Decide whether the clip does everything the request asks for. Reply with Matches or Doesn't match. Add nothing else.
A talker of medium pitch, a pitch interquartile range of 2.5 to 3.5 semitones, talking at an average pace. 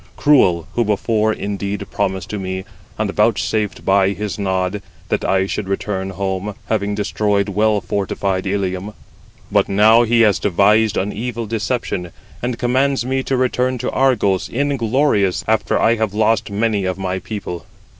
Doesn't match